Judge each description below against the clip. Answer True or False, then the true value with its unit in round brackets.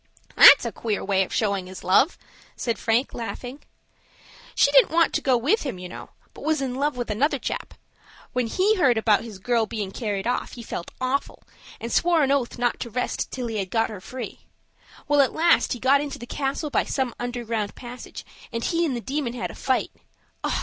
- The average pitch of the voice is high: True (245 Hz)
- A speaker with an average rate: False (210 wpm)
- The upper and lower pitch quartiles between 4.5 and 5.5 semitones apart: False (3.8 semitones)